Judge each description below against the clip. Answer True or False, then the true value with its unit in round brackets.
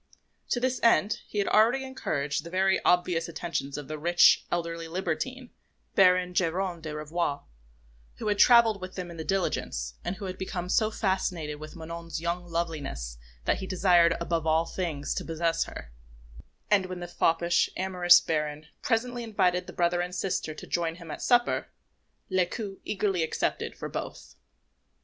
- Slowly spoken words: False (165 wpm)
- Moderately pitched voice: True (175 Hz)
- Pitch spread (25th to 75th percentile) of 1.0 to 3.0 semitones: True (2.7 semitones)